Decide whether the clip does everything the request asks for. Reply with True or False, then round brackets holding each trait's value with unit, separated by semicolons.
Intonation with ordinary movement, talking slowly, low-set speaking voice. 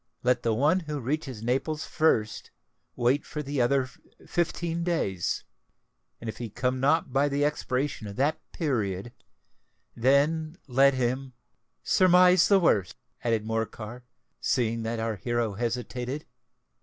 True (4.5 semitones; 130 wpm; 130 Hz)